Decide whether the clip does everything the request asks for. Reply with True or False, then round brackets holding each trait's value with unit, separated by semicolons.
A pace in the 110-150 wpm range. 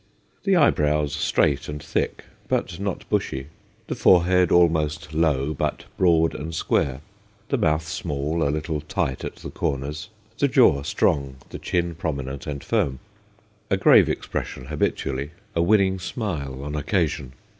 True (145 wpm)